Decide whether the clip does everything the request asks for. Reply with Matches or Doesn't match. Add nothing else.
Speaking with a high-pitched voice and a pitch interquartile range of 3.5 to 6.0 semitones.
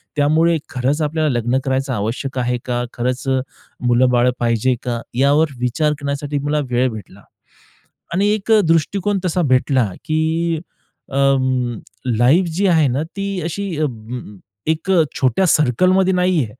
Doesn't match